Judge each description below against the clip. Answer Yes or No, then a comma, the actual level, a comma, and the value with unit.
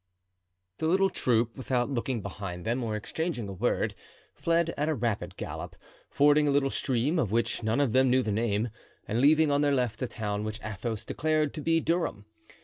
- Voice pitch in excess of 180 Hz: No, low, 125 Hz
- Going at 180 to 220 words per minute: Yes, average, 195 wpm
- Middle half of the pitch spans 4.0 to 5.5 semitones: Yes, average, 5.2 semitones